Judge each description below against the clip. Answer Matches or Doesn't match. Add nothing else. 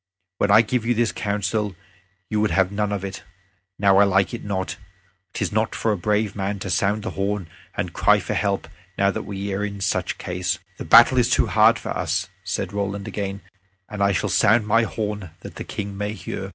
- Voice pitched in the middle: Doesn't match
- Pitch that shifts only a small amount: Matches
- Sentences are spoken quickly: Matches